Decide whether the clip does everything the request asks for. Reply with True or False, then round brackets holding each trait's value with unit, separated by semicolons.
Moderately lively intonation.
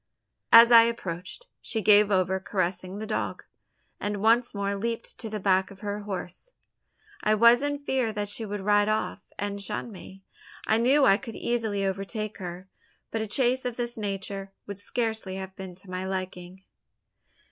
True (3.2 semitones)